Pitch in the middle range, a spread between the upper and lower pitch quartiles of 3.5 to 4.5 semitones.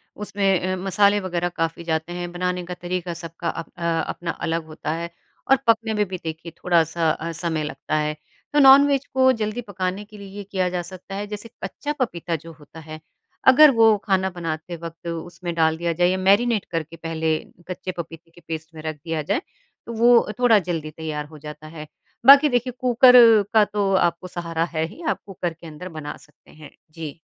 Yes: medium, 175 Hz; average, 4.0 semitones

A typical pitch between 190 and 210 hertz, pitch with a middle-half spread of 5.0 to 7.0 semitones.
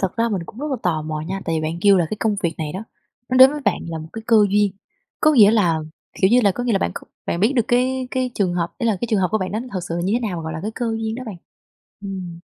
Yes: high, 200 Hz; average, 5.3 semitones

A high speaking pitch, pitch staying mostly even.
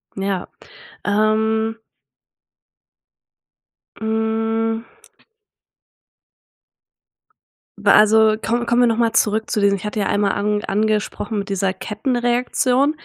Yes: high, 220 Hz; narrow, 1.5 semitones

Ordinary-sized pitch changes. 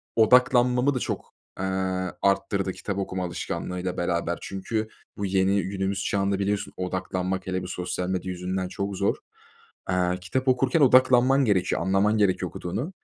Yes: average, 3.2 semitones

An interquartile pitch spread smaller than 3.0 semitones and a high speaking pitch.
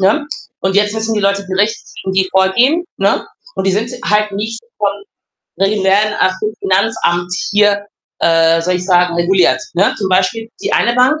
Yes: narrow, 2.4 semitones; high, 200 Hz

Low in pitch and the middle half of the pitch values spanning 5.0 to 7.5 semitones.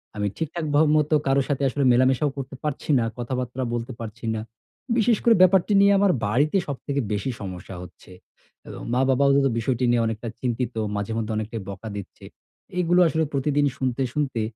No: low, 130 Hz; average, 4.4 semitones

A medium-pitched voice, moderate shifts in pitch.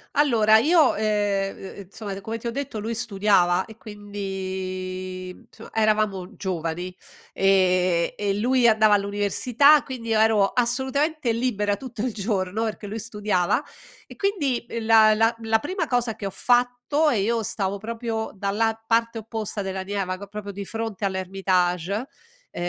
No: high, 215 Hz; average, 3.0 semitones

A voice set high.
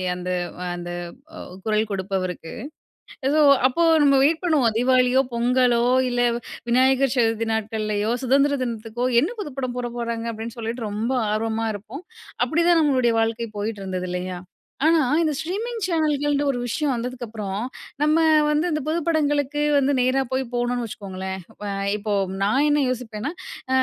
Yes: high, 245 Hz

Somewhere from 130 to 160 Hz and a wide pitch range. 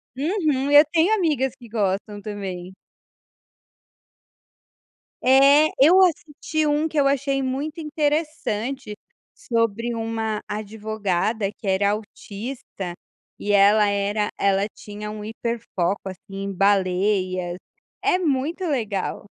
No: high, 220 Hz; wide, 5.8 semitones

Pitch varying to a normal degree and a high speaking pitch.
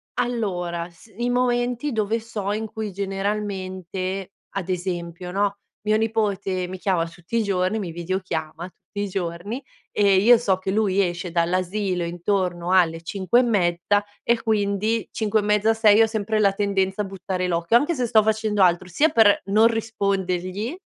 Yes: average, 3.2 semitones; high, 200 Hz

